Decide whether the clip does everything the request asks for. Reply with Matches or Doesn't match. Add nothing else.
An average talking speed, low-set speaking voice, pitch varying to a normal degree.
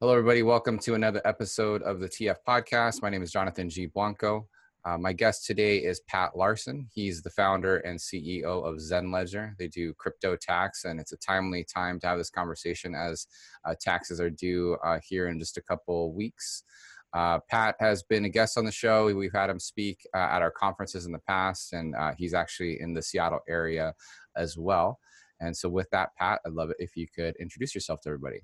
Doesn't match